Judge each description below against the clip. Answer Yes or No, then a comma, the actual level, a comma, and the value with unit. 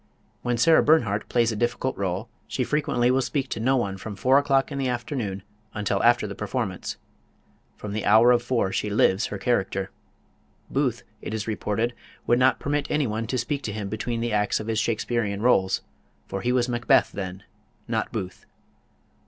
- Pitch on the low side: Yes, low, 115 Hz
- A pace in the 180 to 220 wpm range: Yes, average, 185 wpm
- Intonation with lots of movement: No, average, 3.4 semitones